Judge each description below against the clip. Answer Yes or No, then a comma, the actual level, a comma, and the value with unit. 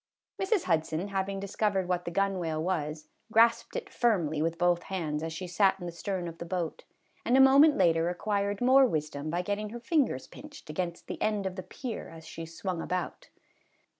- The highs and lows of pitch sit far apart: No, average, 4.2 semitones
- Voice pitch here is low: No, medium, 185 Hz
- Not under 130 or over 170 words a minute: No, average, 195 wpm